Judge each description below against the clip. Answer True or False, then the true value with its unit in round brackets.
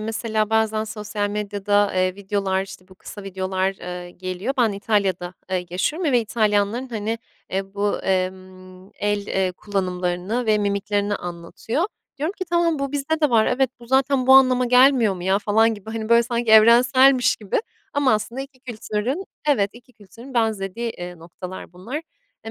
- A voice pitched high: True (210 Hz)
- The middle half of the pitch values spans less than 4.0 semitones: False (4.3 semitones)